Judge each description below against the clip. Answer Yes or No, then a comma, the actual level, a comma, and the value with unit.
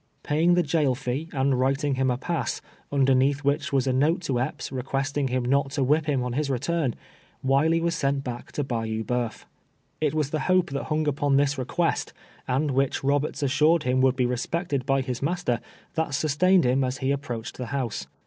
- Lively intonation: No, average, 2.8 semitones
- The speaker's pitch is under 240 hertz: Yes, medium, 140 Hz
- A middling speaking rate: No, fast, 210 wpm